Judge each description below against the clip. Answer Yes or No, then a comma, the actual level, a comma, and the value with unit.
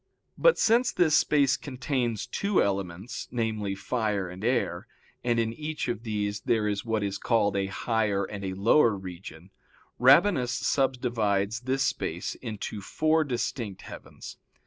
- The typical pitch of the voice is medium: No, low, 110 Hz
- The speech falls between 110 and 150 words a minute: Yes, average, 145 wpm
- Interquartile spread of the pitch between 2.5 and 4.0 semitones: No, average, 4.5 semitones